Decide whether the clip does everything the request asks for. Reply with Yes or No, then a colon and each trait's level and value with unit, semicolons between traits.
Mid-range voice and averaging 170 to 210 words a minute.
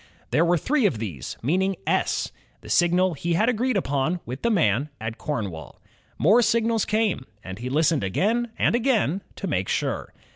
Yes: medium, 175 Hz; average, 175 wpm